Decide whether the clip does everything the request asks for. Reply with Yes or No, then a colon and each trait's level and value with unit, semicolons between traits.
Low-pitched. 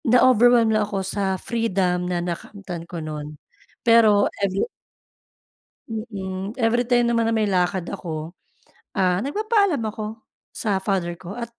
No: high, 200 Hz